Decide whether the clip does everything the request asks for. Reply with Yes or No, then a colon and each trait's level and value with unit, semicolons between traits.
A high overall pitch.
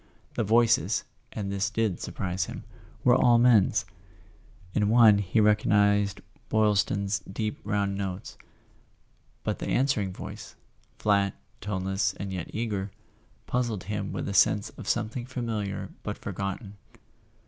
No: low, 105 Hz